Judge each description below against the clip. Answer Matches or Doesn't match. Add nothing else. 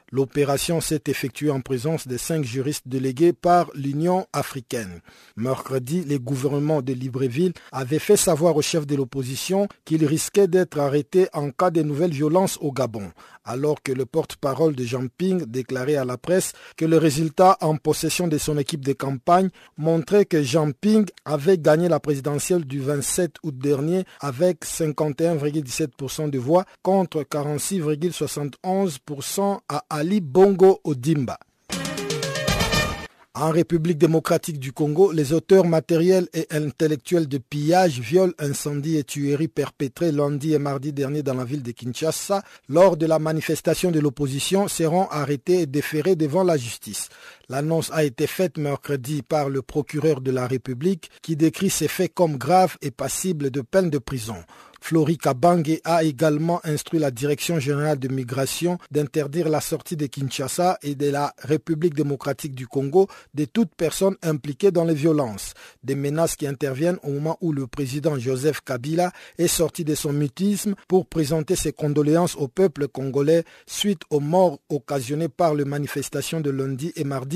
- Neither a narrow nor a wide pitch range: Matches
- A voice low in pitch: Doesn't match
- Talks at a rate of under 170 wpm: Matches